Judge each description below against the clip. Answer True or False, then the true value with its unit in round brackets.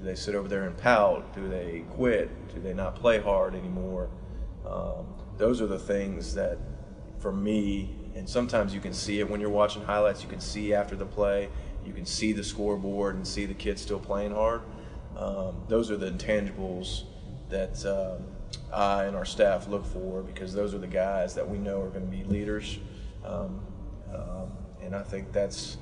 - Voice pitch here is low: True (100 Hz)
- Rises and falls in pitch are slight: True (1.6 semitones)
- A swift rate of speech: False (195 wpm)